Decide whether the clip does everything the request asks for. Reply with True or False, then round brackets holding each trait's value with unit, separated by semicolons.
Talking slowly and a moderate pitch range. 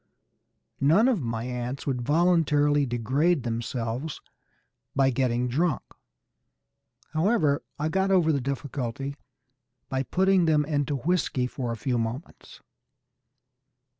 True (110 wpm; 4.4 semitones)